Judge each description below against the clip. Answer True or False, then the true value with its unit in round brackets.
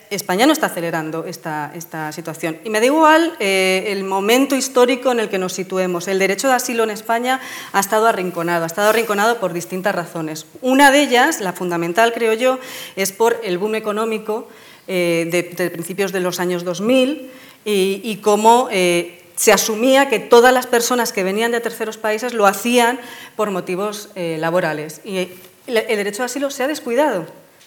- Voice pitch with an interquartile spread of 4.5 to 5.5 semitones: True (4.9 semitones)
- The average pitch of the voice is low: False (210 Hz)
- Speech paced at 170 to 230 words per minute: True (180 wpm)